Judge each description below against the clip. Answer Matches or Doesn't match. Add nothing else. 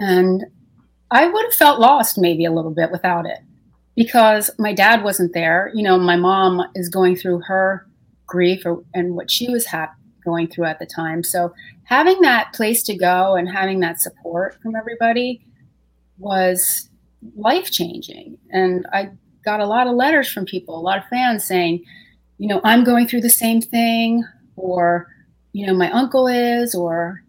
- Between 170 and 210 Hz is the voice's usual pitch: Matches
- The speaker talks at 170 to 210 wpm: Matches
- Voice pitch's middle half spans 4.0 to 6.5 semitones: Matches